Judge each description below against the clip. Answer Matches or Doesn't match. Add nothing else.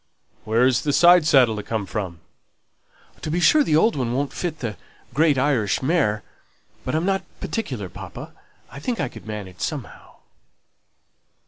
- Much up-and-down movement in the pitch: Matches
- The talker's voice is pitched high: Doesn't match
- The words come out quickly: Doesn't match